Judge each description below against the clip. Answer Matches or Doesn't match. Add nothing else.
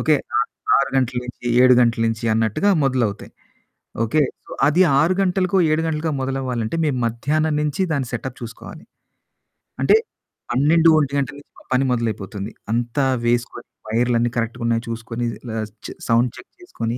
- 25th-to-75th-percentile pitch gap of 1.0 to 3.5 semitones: Doesn't match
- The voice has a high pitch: Doesn't match